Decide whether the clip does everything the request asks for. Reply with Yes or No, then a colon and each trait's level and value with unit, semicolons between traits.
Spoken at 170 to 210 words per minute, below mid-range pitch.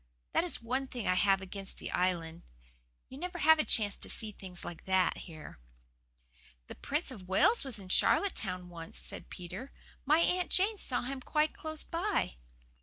No: average, 180 wpm; high, 230 Hz